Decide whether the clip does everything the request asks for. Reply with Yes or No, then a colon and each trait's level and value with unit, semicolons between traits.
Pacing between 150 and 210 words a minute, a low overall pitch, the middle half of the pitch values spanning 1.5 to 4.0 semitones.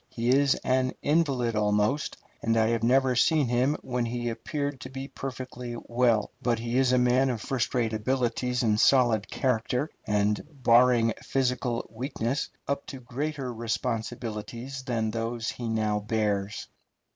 Yes: average, 155 wpm; low, 120 Hz; narrow, 2.5 semitones